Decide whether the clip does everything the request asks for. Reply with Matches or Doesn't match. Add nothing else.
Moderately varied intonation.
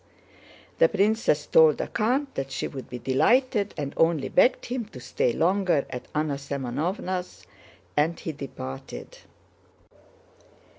Doesn't match